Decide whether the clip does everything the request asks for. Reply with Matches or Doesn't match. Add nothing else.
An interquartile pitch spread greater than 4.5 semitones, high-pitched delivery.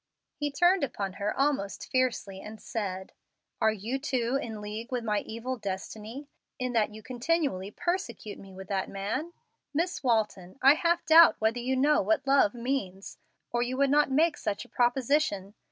Matches